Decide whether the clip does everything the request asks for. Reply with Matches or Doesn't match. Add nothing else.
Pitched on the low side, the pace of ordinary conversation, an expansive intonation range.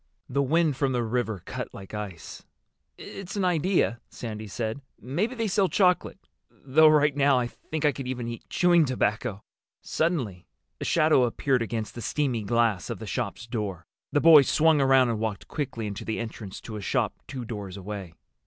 Matches